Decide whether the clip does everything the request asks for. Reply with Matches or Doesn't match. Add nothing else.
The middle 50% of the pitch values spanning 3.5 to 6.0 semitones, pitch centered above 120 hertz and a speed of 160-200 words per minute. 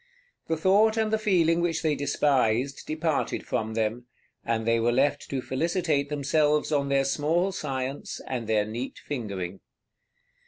Doesn't match